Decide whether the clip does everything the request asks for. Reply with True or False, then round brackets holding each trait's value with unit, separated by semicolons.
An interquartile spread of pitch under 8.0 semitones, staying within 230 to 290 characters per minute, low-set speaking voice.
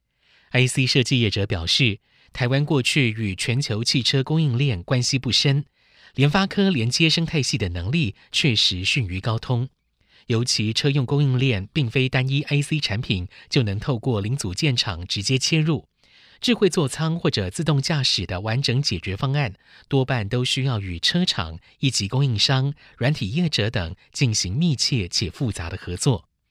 True (5.4 semitones; 255 characters per minute; 130 Hz)